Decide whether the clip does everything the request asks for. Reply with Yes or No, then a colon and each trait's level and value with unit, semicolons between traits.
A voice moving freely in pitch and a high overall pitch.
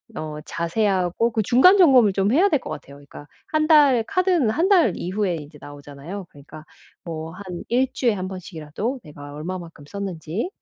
Yes: wide, 8.0 semitones; high, 195 Hz